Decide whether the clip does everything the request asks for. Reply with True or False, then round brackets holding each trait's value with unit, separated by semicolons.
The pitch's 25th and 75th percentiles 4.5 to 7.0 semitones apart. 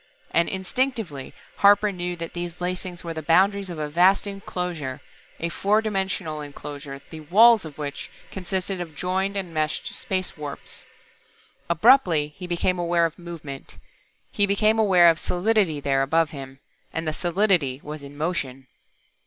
False (4.0 semitones)